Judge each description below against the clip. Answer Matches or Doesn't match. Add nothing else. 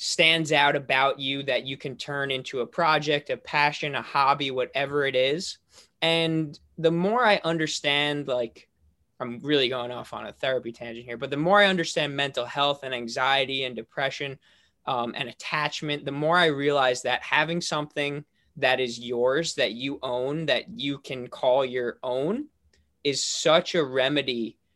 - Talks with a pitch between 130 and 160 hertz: Matches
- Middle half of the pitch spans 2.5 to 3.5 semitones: Matches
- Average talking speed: Matches